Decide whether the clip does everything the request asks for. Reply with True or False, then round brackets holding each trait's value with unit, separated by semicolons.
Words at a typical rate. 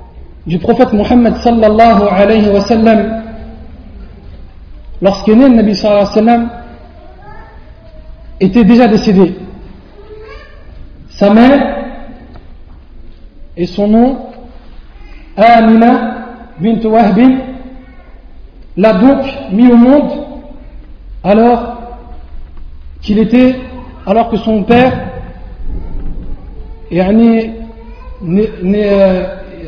False (75 wpm)